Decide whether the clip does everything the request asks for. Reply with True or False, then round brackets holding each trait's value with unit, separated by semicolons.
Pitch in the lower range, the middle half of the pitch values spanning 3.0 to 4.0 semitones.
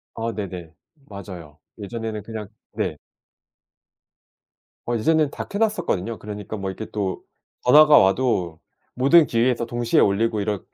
True (110 Hz; 3.5 semitones)